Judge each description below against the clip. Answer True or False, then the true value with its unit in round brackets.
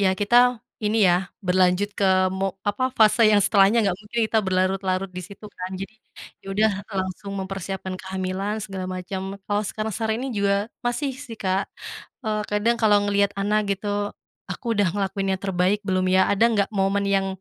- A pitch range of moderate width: False (1.9 semitones)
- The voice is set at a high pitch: True (200 Hz)